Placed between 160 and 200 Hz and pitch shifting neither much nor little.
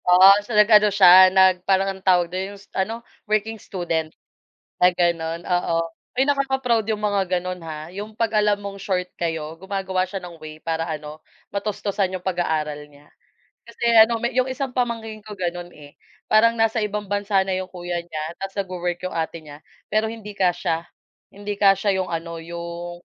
Yes: high, 190 Hz; average, 3.4 semitones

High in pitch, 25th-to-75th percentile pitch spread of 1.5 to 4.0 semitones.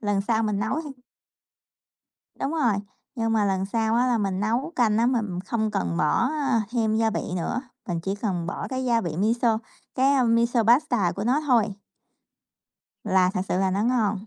Yes: high, 225 Hz; average, 3.5 semitones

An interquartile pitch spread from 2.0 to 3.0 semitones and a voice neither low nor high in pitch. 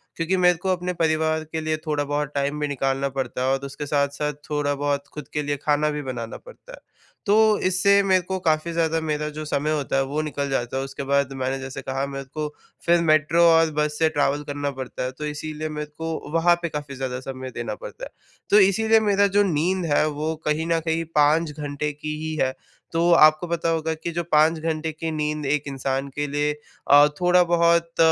Yes: narrow, 2.6 semitones; medium, 150 Hz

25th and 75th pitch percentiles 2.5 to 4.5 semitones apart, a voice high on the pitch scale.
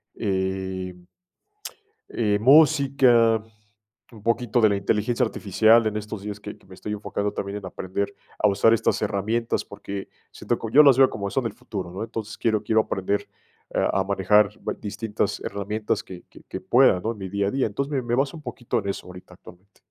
No: average, 2.9 semitones; low, 105 Hz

